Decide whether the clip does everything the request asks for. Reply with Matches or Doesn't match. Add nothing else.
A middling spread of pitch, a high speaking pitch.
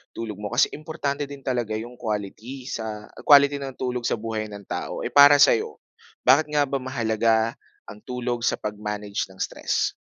Doesn't match